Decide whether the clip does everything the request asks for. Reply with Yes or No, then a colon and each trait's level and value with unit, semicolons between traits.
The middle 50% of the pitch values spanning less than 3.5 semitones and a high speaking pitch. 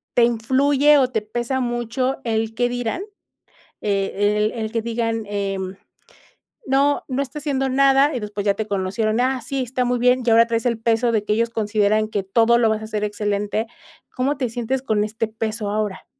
Yes: average, 2.9 semitones; high, 230 Hz